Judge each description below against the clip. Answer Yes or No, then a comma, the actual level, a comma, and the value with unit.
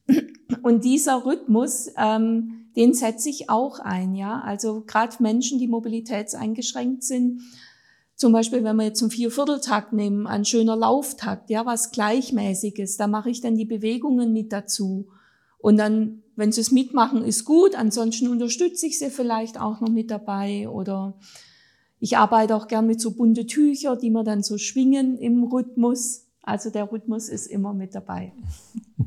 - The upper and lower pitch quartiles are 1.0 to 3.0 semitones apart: Yes, average, 2.7 semitones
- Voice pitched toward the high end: Yes, high, 225 Hz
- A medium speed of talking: Yes, average, 160 wpm